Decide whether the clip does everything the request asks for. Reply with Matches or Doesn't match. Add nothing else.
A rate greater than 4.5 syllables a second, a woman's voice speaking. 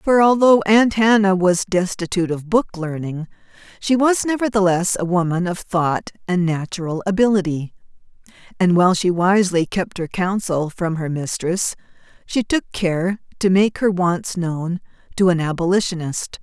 Matches